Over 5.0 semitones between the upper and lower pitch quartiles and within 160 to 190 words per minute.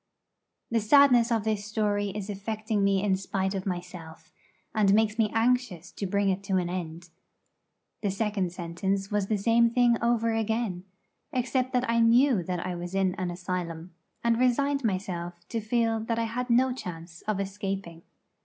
No: average, 3.8 semitones; average, 170 wpm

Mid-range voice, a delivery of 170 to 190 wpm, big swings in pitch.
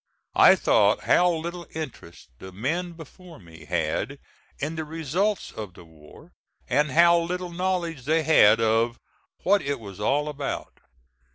No: medium, 150 Hz; average, 150 wpm; wide, 7.5 semitones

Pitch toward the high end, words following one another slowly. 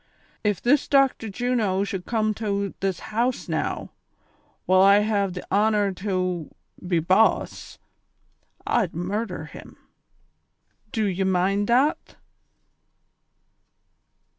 Yes: high, 200 Hz; slow, 105 wpm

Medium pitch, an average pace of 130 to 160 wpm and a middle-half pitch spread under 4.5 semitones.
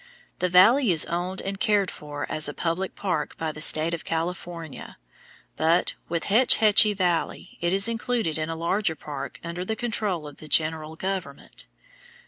No: medium, 170 Hz; average, 170 wpm; average, 3.7 semitones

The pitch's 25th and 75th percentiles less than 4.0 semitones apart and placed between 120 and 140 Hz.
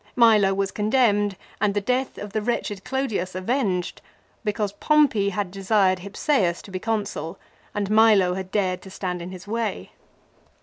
No: average, 2.8 semitones; high, 205 Hz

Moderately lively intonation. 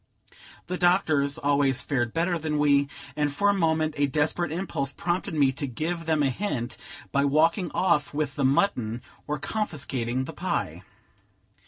Yes: average, 3.2 semitones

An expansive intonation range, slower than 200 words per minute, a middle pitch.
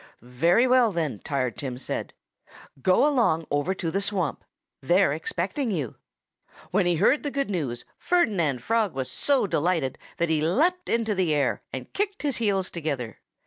Yes: wide, 7.6 semitones; average, 165 wpm; medium, 180 Hz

